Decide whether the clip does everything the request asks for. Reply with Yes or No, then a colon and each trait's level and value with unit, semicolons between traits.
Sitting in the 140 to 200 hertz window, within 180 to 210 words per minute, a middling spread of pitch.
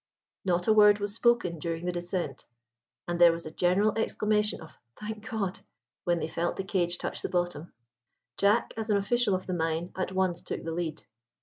Yes: medium, 185 Hz; average, 195 wpm; average, 3.3 semitones